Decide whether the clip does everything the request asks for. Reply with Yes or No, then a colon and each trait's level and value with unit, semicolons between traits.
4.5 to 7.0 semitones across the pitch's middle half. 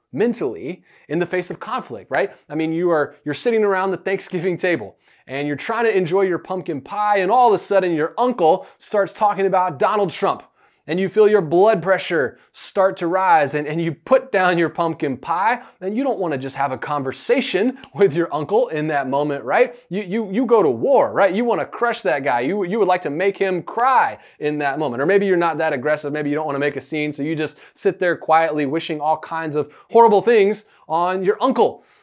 Yes: average, 4.8 semitones